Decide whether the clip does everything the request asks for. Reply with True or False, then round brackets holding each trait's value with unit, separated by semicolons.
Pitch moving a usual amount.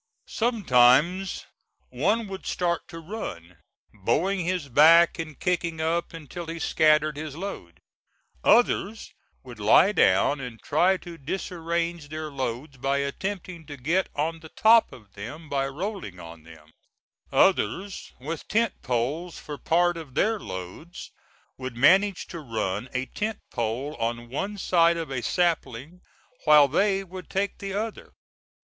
False (6.0 semitones)